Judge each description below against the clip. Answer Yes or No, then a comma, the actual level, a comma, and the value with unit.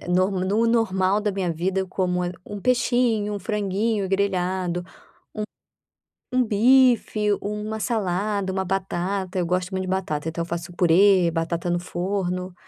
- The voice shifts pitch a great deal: No, average, 2.7 semitones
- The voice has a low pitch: No, high, 190 Hz